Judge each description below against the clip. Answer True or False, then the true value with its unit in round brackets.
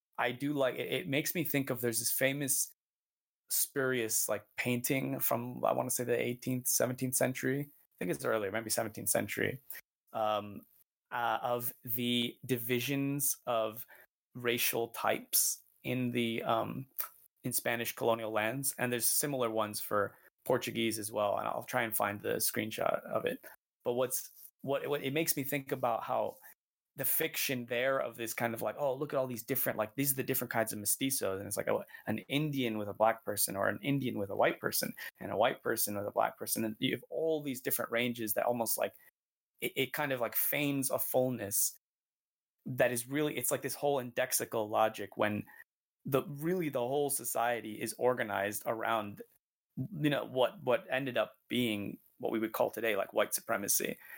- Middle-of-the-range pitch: False (120 Hz)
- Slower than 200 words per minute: True (190 wpm)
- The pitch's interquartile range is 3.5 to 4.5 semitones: False (3.1 semitones)